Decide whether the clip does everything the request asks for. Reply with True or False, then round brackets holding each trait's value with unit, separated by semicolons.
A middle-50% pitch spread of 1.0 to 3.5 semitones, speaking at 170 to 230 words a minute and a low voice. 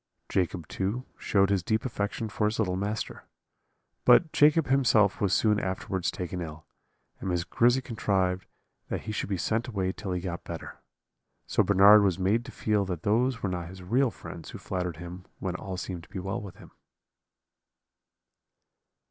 True (3.1 semitones; 175 wpm; 95 Hz)